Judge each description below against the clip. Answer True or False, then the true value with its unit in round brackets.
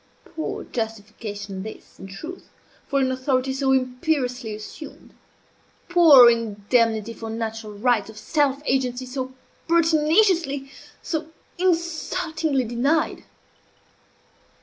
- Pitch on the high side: True (260 Hz)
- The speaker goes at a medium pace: False (100 wpm)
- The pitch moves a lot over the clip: True (5.7 semitones)